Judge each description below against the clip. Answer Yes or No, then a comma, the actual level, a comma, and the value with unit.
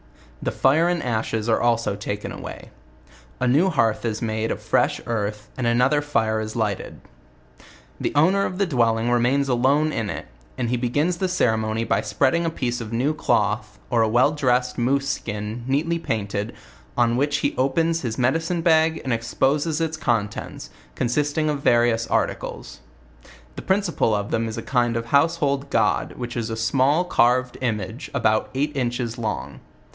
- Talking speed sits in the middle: Yes, average, 175 wpm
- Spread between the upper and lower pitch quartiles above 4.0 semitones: Yes, average, 4.6 semitones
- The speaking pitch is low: Yes, low, 125 Hz